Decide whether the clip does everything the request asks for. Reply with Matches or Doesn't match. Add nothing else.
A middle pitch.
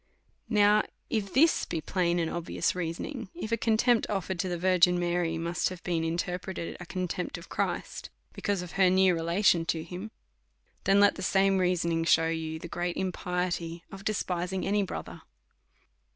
Matches